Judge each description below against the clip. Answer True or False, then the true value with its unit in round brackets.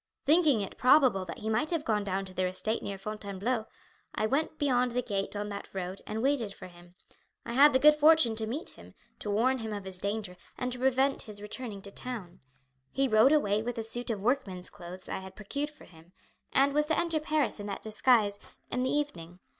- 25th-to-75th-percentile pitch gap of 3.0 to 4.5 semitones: False (5.1 semitones)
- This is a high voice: True (220 Hz)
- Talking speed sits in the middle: False (225 wpm)